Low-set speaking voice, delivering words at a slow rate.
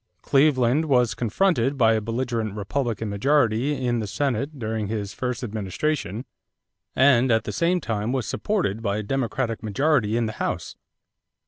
No: low, 120 Hz; average, 150 wpm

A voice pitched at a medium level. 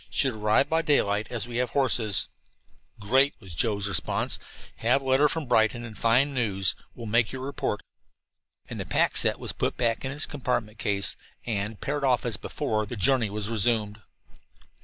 No: low, 115 Hz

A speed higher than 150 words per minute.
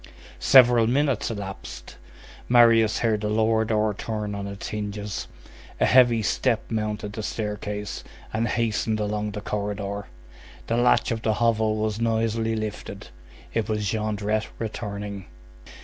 No: slow, 135 wpm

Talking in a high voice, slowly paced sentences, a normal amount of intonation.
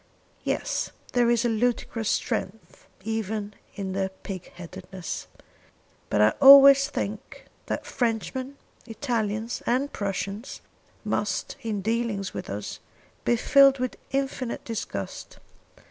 Yes: high, 225 Hz; slow, 115 wpm; average, 4.0 semitones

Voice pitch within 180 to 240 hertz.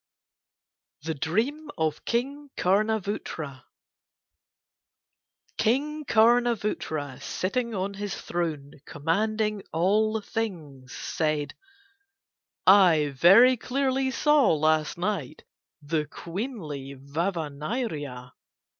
Yes: medium, 185 Hz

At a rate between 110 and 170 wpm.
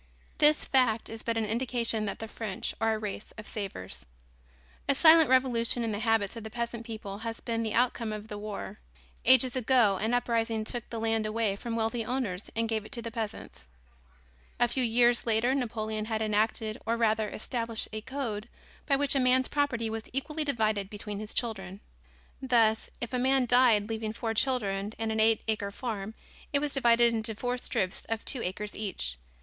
No: average, 190 wpm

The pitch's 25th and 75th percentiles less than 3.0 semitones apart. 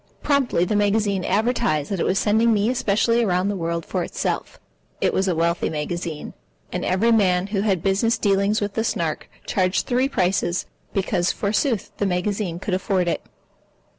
No: average, 3.3 semitones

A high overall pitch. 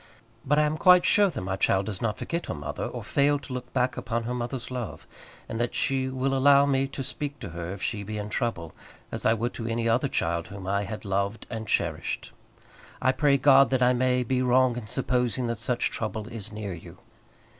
No: low, 120 Hz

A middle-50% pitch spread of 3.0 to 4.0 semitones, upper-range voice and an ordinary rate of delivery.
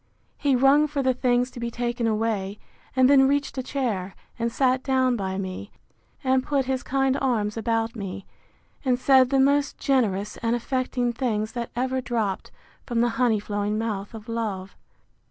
Yes: average, 3.3 semitones; high, 240 Hz; average, 170 wpm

